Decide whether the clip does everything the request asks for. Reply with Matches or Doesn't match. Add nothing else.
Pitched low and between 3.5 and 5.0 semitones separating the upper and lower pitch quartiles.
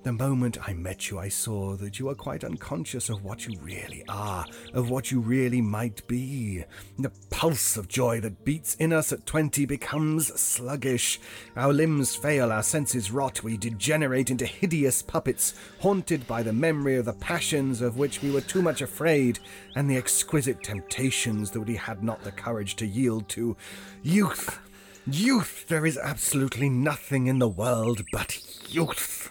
Matches